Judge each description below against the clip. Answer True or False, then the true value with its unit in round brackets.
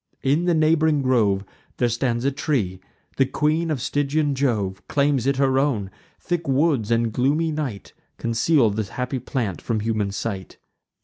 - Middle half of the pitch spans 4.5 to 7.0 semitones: True (4.8 semitones)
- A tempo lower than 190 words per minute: True (160 wpm)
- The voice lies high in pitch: False (130 Hz)